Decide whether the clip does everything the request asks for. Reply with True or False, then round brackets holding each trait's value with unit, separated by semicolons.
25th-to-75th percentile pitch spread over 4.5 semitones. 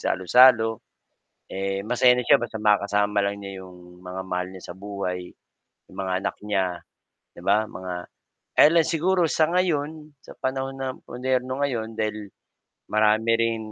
True (5.0 semitones)